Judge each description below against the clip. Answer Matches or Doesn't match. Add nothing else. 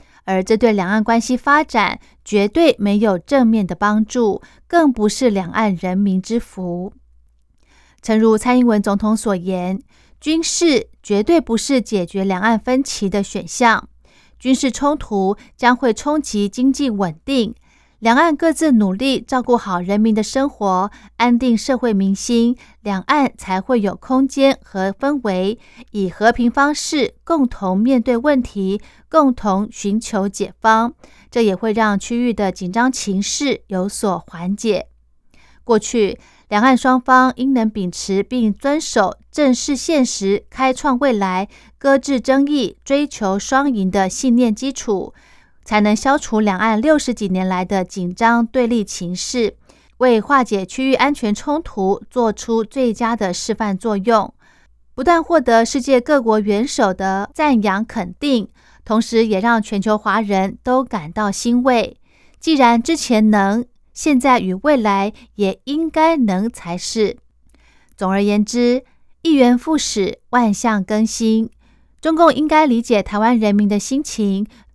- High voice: Matches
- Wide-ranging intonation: Doesn't match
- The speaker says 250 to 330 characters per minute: Doesn't match